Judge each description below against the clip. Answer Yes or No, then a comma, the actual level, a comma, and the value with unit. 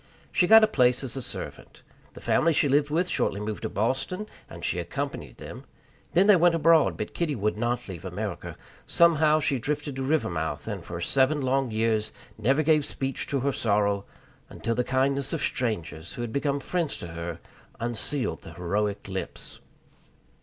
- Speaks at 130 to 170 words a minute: No, average, 180 wpm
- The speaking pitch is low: Yes, low, 130 Hz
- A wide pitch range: Yes, wide, 6.0 semitones